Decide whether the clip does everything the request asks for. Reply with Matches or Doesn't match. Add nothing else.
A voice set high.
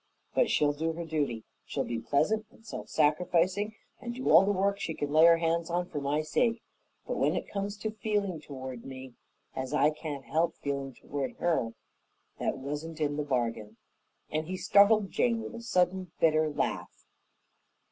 Doesn't match